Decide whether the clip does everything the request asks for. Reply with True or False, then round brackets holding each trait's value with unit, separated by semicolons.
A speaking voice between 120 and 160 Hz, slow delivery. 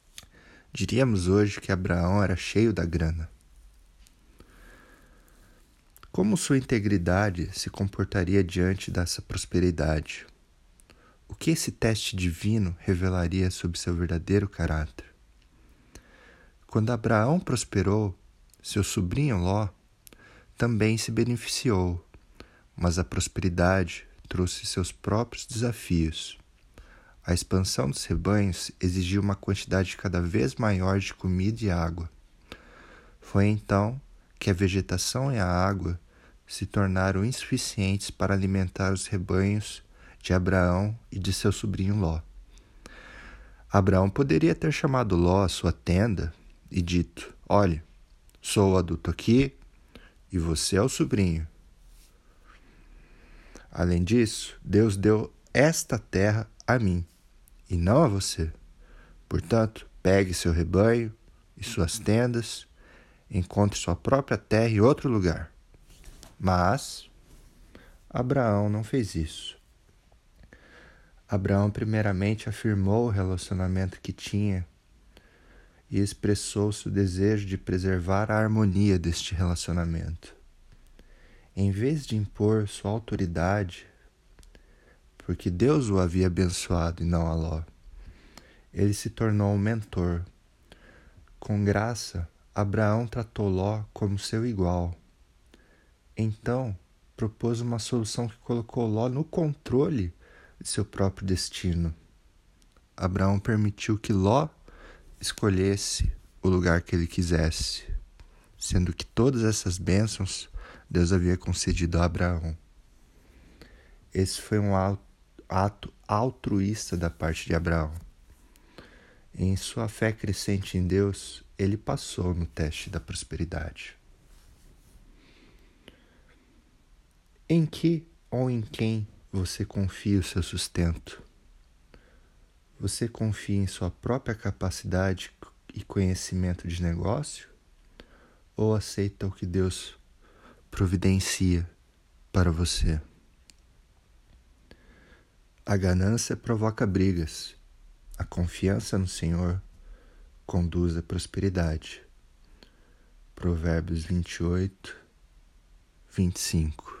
False (95 Hz; 105 wpm)